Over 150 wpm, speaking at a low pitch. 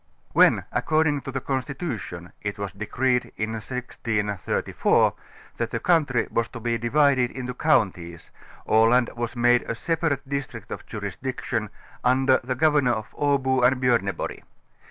No: average, 140 wpm; low, 125 Hz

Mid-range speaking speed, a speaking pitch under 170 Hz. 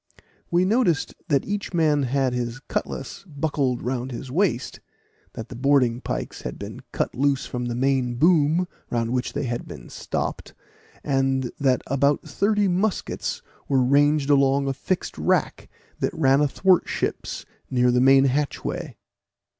Yes: average, 150 wpm; low, 135 Hz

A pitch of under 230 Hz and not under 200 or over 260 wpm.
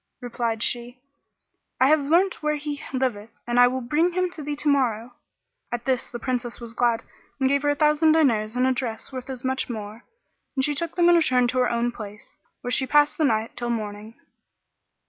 No: very high, 255 Hz; fast, 205 wpm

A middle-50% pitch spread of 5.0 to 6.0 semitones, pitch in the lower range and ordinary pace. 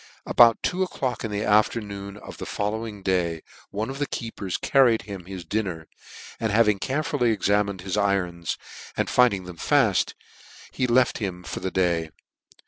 No: average, 3.7 semitones; low, 105 Hz; average, 170 wpm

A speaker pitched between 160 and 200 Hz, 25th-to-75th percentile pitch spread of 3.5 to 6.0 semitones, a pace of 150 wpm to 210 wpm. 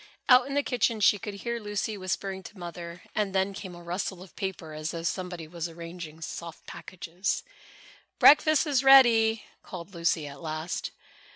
Yes: medium, 185 Hz; average, 4.0 semitones; average, 170 wpm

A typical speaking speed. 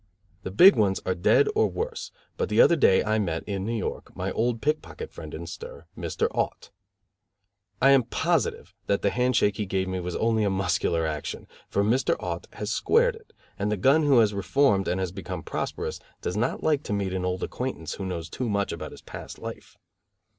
No: fast, 210 wpm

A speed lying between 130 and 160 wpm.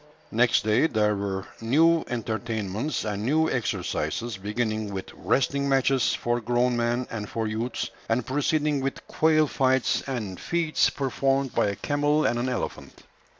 Yes: average, 150 wpm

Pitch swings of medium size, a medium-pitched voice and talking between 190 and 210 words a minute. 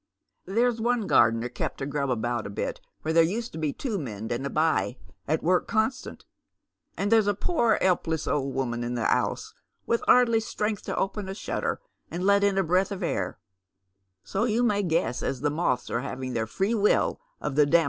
No: wide, 7.9 semitones; medium, 175 Hz; fast, 205 wpm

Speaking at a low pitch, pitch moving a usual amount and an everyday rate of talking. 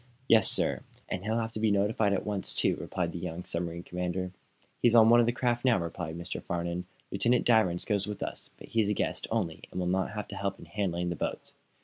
No: very low, 95 Hz; average, 4.0 semitones; fast, 235 wpm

